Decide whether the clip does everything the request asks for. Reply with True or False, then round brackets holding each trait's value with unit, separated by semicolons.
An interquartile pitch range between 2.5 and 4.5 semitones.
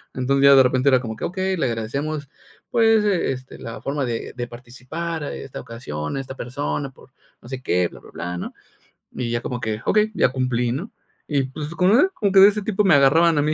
False (5.6 semitones)